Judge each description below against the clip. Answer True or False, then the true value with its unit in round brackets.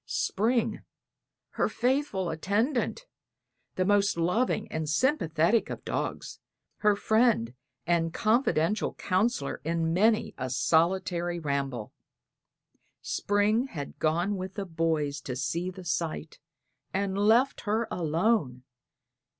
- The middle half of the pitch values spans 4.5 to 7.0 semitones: True (5.1 semitones)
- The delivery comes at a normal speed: False (110 wpm)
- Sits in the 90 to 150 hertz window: False (185 Hz)